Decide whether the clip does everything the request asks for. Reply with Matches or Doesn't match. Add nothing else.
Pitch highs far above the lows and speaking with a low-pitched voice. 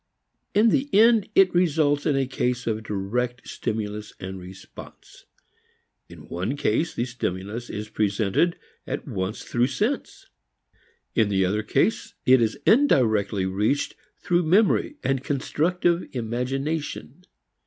Matches